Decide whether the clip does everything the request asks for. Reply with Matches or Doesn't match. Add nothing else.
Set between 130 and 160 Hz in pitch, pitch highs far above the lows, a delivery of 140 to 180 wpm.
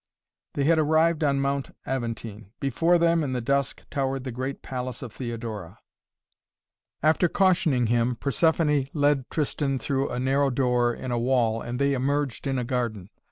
Doesn't match